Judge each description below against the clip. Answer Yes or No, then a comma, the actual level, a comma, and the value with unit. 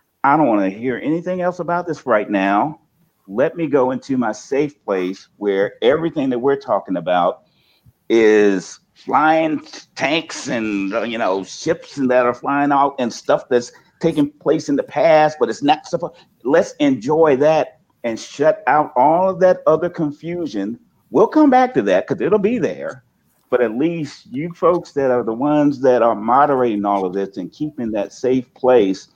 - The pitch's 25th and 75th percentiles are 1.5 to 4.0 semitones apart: No, wide, 5.6 semitones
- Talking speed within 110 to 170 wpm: No, average, 180 wpm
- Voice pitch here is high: No, medium, 150 Hz